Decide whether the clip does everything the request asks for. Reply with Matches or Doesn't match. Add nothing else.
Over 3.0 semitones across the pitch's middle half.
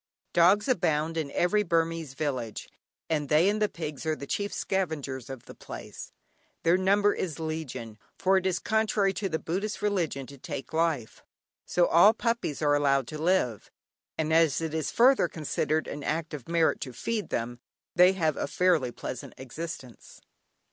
Matches